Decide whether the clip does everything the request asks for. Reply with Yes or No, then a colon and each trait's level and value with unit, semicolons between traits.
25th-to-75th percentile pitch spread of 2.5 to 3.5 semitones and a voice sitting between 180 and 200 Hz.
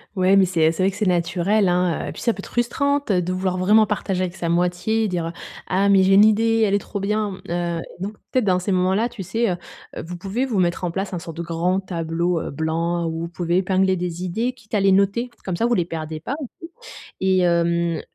Yes: average, 3.0 semitones; medium, 185 Hz